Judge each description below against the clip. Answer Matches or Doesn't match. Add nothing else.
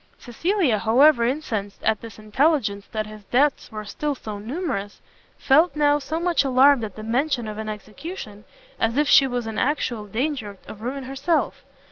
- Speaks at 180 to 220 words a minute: Doesn't match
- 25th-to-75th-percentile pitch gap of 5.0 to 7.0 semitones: Matches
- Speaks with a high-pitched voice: Matches